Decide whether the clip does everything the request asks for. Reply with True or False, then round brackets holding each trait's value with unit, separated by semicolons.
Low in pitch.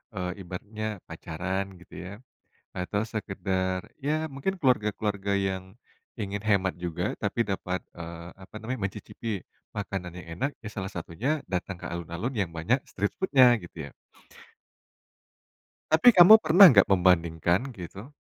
True (95 Hz)